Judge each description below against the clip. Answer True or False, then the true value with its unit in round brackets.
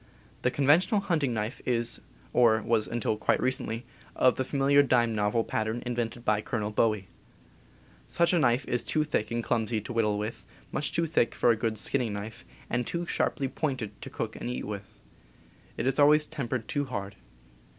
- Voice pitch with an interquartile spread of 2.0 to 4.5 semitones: True (4.1 semitones)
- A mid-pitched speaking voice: False (120 Hz)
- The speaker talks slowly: False (180 wpm)